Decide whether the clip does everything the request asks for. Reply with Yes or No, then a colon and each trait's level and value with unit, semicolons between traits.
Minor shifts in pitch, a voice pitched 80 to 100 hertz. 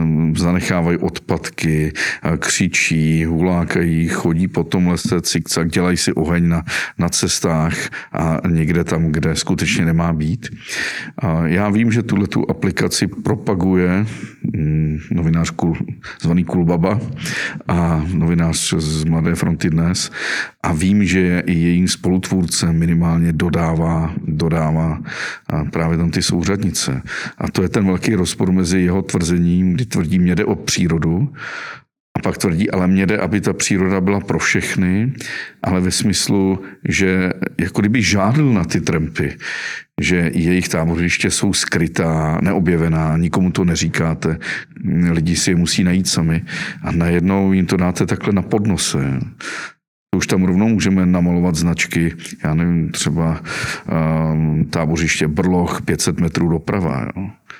Yes: narrow, 2.0 semitones; very low, 85 Hz